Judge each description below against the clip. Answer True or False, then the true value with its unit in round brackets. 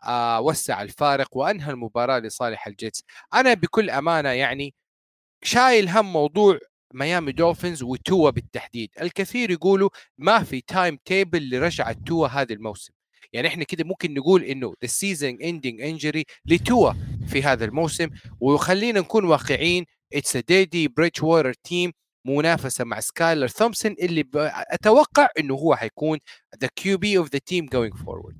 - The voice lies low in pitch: False (155 Hz)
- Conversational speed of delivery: False (140 wpm)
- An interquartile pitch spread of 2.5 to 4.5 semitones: False (5.6 semitones)